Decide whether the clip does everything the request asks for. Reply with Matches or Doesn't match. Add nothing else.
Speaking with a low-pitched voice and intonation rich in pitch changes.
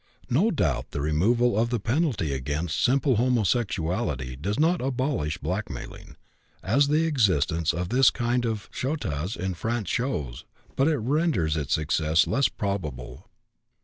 Matches